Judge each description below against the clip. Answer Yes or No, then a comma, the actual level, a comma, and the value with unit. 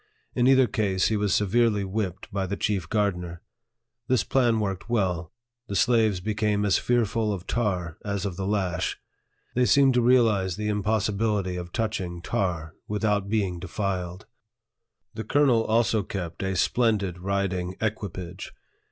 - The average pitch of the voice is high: No, low, 100 Hz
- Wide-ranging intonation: No, average, 3.1 semitones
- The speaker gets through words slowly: No, average, 145 wpm